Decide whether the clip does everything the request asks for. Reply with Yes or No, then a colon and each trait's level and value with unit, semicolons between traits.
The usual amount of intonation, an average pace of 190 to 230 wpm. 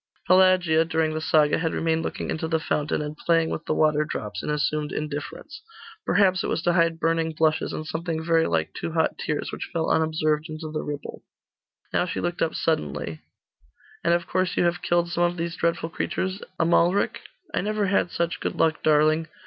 No: narrow, 1.8 semitones; average, 195 wpm